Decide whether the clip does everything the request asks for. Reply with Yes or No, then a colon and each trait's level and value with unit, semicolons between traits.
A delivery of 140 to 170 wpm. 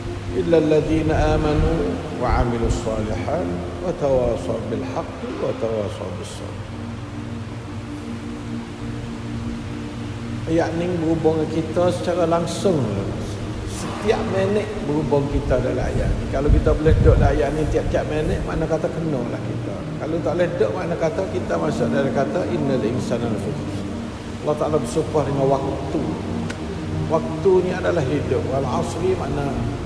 No: average, 130 wpm